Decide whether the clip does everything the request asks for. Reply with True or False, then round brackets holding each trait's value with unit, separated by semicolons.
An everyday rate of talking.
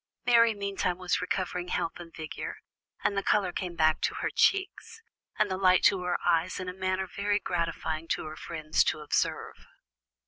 True (180 wpm)